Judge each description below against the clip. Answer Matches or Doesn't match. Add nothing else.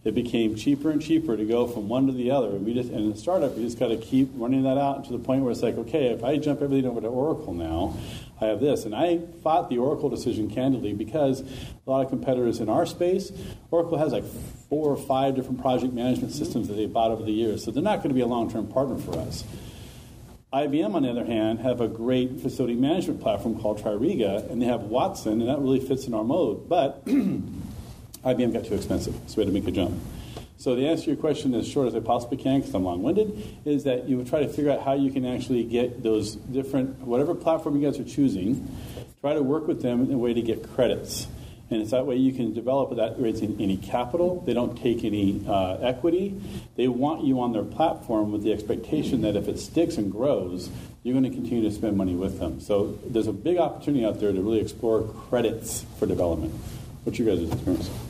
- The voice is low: Matches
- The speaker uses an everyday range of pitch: Matches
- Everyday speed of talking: Doesn't match